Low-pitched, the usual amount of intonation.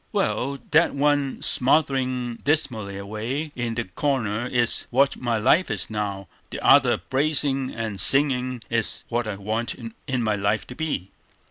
Yes: low, 120 Hz; average, 4.1 semitones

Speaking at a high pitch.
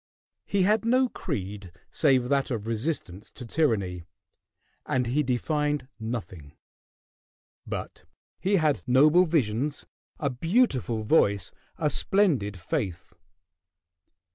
No: low, 130 Hz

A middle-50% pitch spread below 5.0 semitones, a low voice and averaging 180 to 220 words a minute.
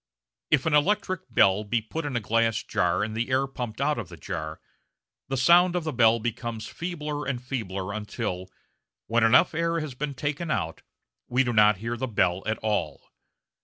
No: wide, 5.5 semitones; low, 120 Hz; average, 195 wpm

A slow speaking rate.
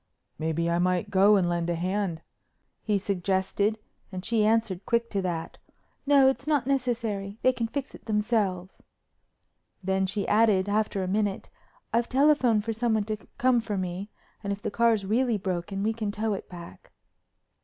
No: average, 170 wpm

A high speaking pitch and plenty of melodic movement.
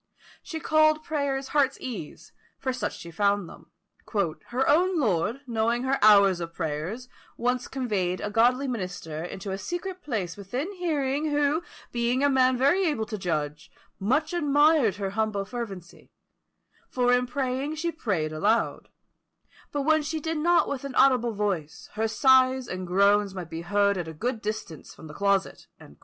Yes: high, 240 Hz; wide, 6.2 semitones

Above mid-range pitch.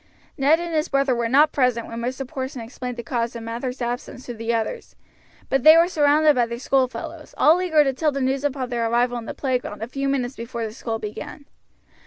Yes: very high, 255 Hz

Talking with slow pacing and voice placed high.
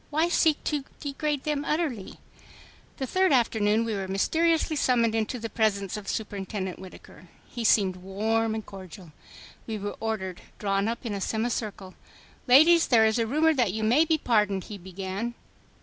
No: average, 170 wpm; high, 220 Hz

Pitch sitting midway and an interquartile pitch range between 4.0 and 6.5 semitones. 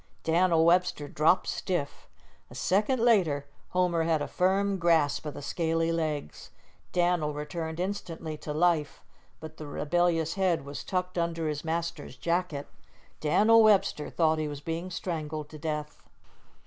No: medium, 165 Hz; average, 2.9 semitones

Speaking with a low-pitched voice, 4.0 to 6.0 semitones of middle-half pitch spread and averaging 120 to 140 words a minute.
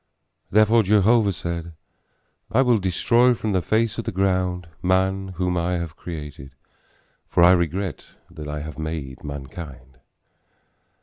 Yes: very low, 90 Hz; average, 4.3 semitones; slow, 135 wpm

